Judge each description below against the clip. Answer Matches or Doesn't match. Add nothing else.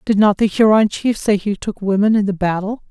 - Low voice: Doesn't match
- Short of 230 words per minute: Doesn't match